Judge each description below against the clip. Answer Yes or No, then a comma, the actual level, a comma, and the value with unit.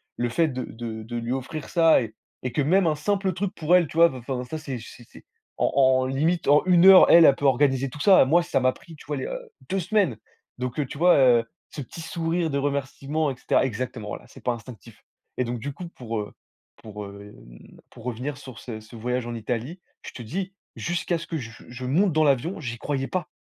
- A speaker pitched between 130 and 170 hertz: Yes, low, 135 Hz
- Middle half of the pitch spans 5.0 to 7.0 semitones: Yes, wide, 5.4 semitones